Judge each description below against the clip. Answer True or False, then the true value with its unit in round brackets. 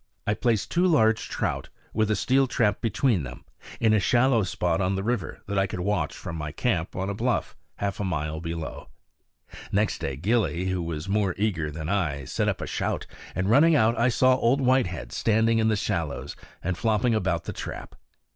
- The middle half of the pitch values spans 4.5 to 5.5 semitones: True (4.9 semitones)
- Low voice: True (100 Hz)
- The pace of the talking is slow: False (200 wpm)